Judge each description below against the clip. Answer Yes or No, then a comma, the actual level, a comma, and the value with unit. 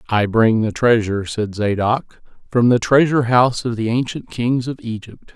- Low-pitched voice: Yes, low, 115 Hz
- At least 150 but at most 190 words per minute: Yes, average, 180 wpm